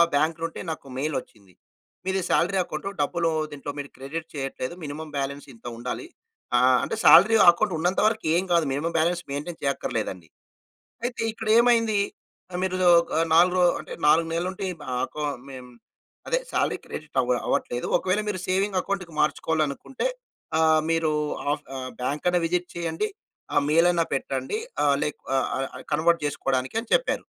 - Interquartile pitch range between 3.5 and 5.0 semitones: Yes, average, 4.4 semitones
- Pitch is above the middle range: No, medium, 165 Hz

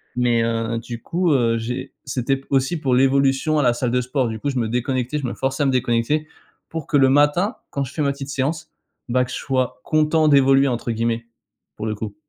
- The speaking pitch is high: No, low, 130 Hz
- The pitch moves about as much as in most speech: Yes, average, 3.1 semitones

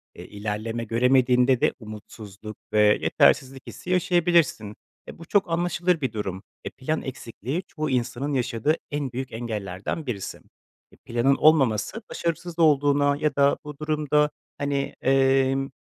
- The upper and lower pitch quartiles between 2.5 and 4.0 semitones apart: No, average, 4.8 semitones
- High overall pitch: No, low, 135 Hz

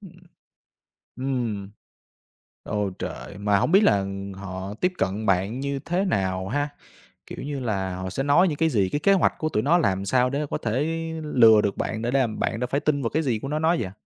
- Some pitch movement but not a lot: No, wide, 6.7 semitones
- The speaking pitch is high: No, low, 120 Hz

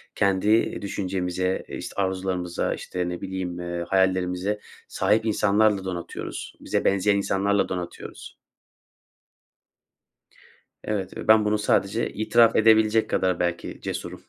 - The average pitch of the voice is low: Yes, very low, 95 Hz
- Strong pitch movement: No, narrow, 2.6 semitones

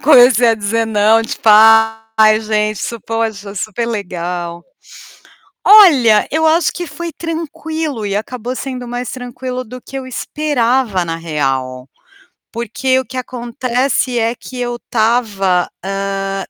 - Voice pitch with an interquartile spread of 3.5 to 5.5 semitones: Yes, average, 4.0 semitones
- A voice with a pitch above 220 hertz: Yes, high, 230 Hz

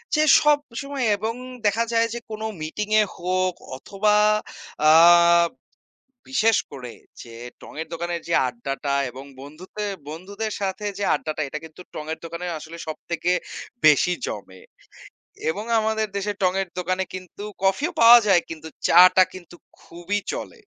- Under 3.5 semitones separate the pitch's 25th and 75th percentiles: No, average, 4.8 semitones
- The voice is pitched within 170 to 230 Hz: Yes, medium, 185 Hz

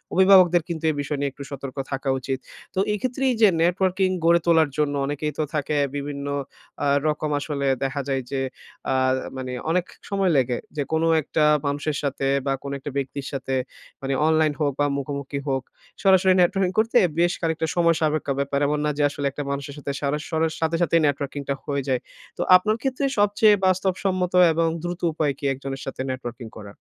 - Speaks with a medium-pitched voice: Yes, medium, 150 Hz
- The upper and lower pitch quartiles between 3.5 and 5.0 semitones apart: Yes, average, 3.9 semitones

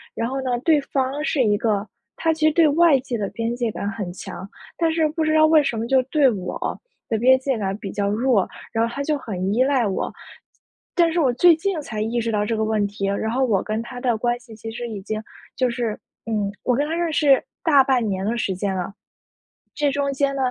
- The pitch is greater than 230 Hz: Yes, high, 240 Hz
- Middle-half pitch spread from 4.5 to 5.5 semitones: Yes, average, 4.8 semitones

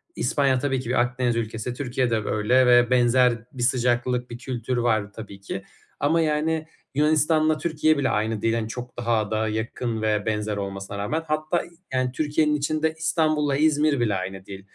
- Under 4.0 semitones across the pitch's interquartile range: No, average, 5.2 semitones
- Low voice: Yes, low, 125 Hz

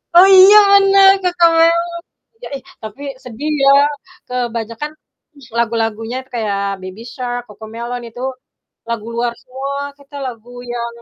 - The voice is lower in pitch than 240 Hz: No, high, 245 Hz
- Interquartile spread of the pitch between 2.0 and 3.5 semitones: No, average, 5.0 semitones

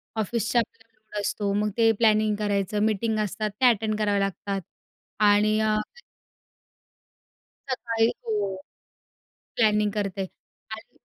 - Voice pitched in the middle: No, high, 215 Hz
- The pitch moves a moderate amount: No, narrow, 1.4 semitones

